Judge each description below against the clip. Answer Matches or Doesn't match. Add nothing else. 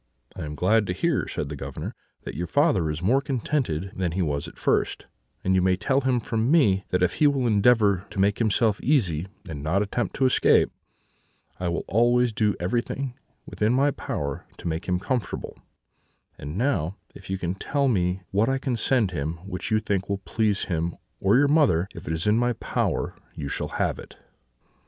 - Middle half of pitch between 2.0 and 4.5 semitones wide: Doesn't match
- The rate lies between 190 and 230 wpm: Matches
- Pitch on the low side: Matches